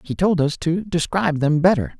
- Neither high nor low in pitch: Yes, medium, 160 Hz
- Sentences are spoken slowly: No, fast, 210 wpm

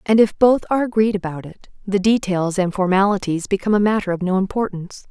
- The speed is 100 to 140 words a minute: No, average, 200 wpm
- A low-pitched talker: No, high, 195 Hz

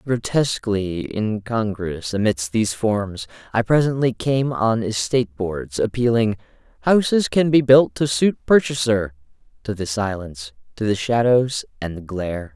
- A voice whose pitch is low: Yes, low, 110 Hz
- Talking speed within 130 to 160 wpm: Yes, slow, 135 wpm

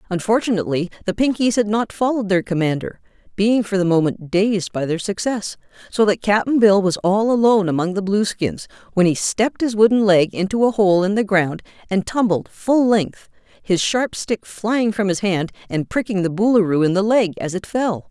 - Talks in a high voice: Yes, high, 200 Hz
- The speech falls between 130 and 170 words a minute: No, average, 195 wpm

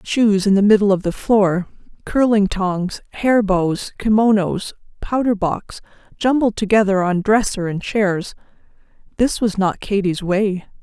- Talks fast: No, slow, 135 wpm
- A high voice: Yes, high, 200 Hz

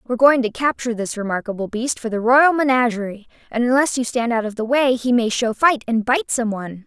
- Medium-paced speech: No, fast, 235 wpm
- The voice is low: No, high, 240 Hz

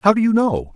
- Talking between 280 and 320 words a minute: Yes, fast, 315 wpm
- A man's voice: Yes, male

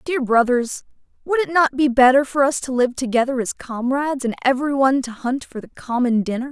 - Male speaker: No, female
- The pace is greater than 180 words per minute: Yes, fast, 205 wpm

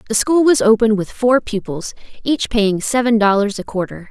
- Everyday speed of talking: Yes, average, 190 wpm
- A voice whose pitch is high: Yes, high, 220 Hz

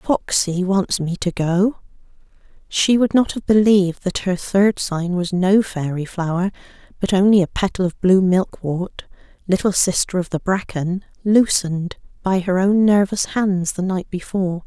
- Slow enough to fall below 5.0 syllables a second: Yes, 4.4 syllables/s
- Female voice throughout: Yes, female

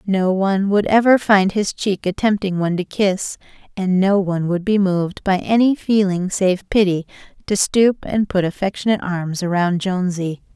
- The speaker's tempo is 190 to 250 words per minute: No, average, 175 wpm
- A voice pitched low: No, high, 190 Hz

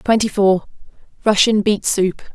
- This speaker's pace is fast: No, slow, 100 wpm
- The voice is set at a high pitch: Yes, high, 205 Hz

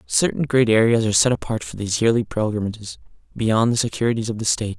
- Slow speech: No, average, 200 wpm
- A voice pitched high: No, low, 115 Hz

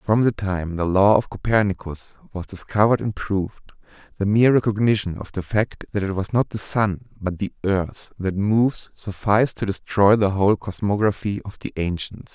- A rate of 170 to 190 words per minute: Yes, average, 180 wpm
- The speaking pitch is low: Yes, low, 100 Hz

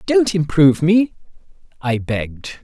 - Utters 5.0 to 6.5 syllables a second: No, 4.6 syllables/s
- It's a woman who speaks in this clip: No, male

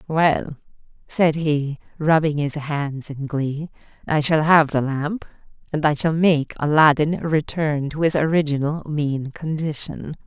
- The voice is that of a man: No, female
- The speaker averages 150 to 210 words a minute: No, average, 140 wpm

